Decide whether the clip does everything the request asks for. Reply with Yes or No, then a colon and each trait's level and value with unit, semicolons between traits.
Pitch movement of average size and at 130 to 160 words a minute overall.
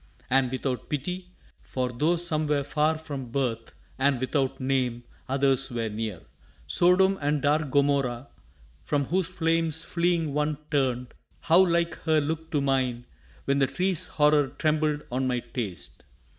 Yes: average, 3.7 semitones; average, 145 wpm